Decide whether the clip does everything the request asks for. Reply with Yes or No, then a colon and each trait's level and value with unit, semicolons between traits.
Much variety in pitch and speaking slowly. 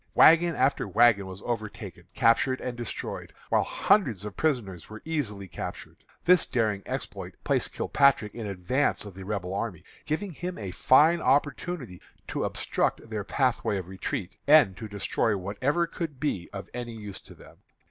No: wide, 6.5 semitones; average, 160 wpm